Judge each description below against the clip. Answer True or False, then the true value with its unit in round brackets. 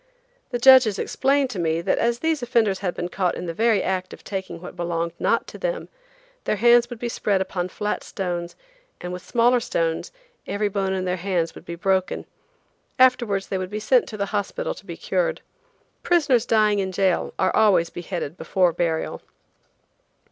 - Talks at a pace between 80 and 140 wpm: False (185 wpm)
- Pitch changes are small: False (4.8 semitones)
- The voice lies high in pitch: True (195 Hz)